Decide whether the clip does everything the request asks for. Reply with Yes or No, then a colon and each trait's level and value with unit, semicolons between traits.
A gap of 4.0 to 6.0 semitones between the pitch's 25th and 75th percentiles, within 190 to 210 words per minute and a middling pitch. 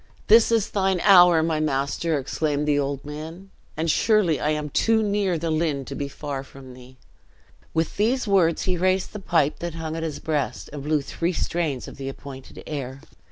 Yes: average, 4.3 semitones; average, 195 wpm; medium, 160 Hz